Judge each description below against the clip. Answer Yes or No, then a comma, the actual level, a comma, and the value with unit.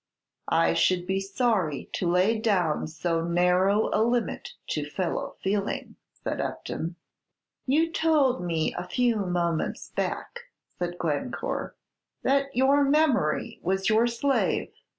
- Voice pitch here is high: Yes, high, 195 Hz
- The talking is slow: Yes, slow, 125 wpm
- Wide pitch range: Yes, wide, 6.0 semitones